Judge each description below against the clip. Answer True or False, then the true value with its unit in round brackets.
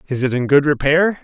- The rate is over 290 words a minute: False (245 wpm)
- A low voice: False (145 Hz)